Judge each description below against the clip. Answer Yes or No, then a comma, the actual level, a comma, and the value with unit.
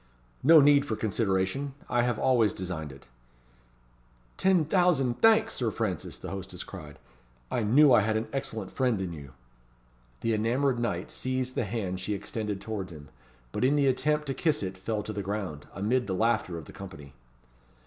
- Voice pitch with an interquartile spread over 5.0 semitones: Yes, wide, 5.6 semitones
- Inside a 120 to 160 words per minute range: No, average, 180 wpm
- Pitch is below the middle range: Yes, low, 110 Hz